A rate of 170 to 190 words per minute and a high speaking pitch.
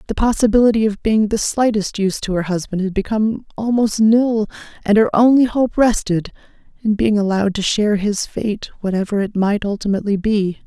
Yes: average, 175 wpm; high, 210 Hz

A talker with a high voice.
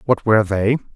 No: low, 110 Hz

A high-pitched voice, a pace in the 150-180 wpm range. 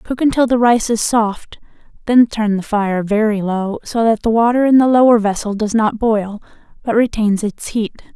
No: high, 220 Hz; average, 200 wpm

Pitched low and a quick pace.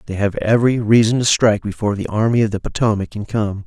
Yes: low, 105 Hz; fast, 230 wpm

